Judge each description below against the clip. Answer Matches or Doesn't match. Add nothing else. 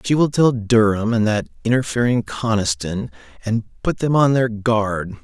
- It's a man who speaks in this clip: Matches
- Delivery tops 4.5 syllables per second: Doesn't match